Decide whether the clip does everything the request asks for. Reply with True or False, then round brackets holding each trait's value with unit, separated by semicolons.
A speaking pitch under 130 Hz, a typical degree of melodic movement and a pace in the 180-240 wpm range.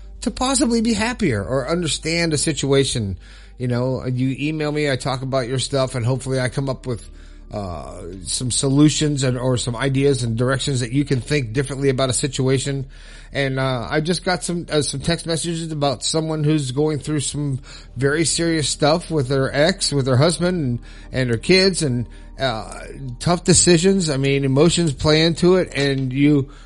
False (140 Hz; 3.5 semitones; 185 wpm)